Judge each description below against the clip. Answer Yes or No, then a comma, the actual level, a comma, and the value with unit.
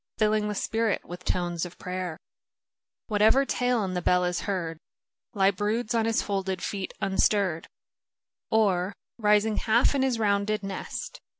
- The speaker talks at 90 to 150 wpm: Yes, average, 145 wpm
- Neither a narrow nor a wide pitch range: Yes, average, 3.1 semitones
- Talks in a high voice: Yes, high, 200 Hz